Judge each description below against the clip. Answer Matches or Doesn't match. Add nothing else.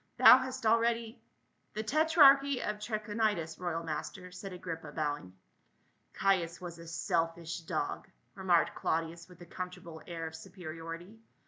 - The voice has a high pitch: Doesn't match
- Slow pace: Doesn't match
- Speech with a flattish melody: Doesn't match